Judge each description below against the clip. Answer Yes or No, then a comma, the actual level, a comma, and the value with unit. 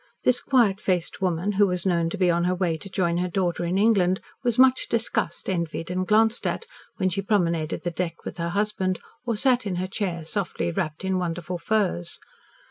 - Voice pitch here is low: No, medium, 185 Hz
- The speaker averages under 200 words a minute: No, fast, 205 wpm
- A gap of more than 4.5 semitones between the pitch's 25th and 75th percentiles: No, average, 3.1 semitones